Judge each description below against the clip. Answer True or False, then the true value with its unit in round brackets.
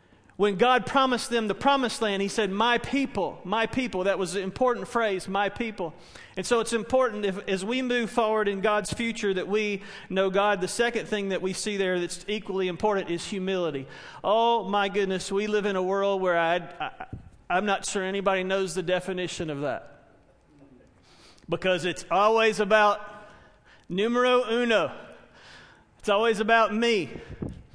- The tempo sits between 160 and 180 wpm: True (170 wpm)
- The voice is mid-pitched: False (200 Hz)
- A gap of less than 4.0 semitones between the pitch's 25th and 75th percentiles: True (3.2 semitones)